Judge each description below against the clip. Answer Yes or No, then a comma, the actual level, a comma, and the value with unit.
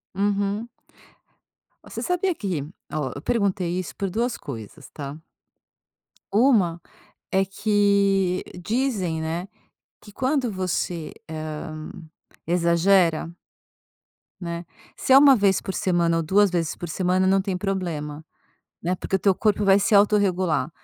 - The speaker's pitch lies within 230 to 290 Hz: No, medium, 185 Hz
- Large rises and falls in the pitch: No, average, 3.2 semitones